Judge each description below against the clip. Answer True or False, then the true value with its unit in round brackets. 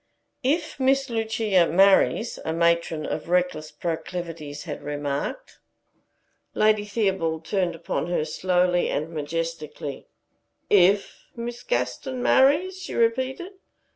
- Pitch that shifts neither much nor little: False (6.4 semitones)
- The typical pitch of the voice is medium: True (180 Hz)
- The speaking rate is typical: False (110 wpm)